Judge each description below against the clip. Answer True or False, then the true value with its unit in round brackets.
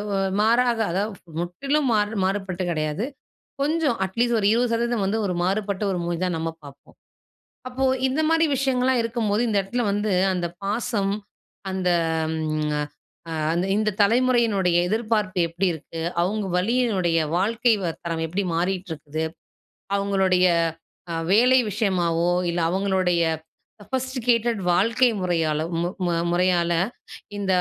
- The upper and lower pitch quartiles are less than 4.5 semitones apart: False (4.8 semitones)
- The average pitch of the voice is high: True (200 Hz)